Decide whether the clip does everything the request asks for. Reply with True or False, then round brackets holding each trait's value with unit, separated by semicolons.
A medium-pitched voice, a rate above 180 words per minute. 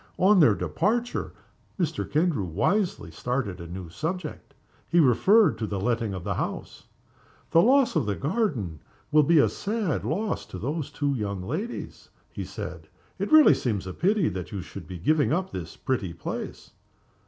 False (145 Hz; 175 wpm)